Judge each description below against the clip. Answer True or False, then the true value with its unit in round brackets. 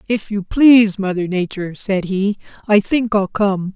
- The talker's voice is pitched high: True (200 Hz)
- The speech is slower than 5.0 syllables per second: True (4.6 syllables/s)